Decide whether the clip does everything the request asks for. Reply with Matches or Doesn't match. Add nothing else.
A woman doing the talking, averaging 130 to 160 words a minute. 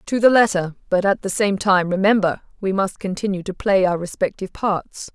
Doesn't match